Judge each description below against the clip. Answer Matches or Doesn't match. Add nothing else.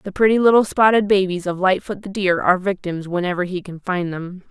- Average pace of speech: Doesn't match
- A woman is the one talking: Matches